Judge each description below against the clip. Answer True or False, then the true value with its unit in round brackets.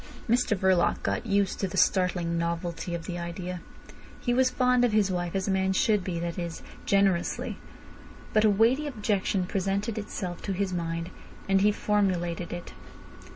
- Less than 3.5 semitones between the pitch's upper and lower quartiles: True (3.1 semitones)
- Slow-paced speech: False (165 wpm)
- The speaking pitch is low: False (190 Hz)